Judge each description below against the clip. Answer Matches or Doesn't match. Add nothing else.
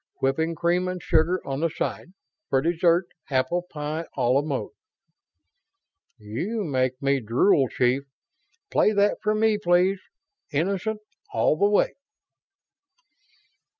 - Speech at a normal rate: Doesn't match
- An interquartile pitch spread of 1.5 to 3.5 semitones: Doesn't match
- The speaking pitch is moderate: Matches